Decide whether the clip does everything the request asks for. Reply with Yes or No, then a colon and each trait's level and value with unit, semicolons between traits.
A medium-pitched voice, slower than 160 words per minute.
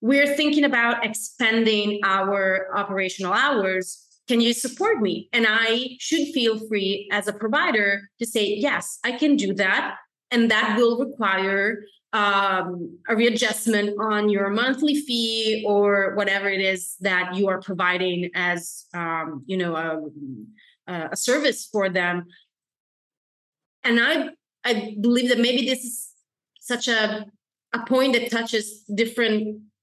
No: high, 215 Hz; average, 140 wpm